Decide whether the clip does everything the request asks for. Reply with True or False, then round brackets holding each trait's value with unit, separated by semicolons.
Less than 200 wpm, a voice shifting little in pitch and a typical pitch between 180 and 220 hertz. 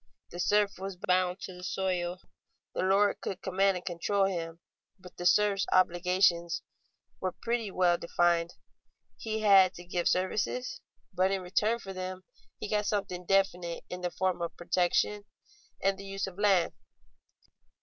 True (155 wpm; 1.9 semitones; 185 Hz)